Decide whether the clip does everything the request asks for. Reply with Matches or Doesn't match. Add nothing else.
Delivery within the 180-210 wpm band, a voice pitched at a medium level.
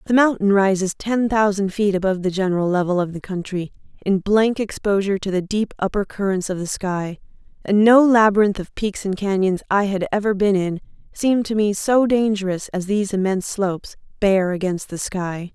Doesn't match